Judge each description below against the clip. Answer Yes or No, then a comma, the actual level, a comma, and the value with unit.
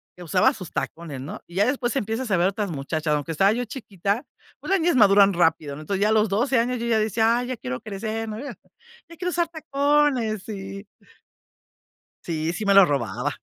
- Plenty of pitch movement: Yes, wide, 5.9 semitones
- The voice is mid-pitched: No, high, 210 Hz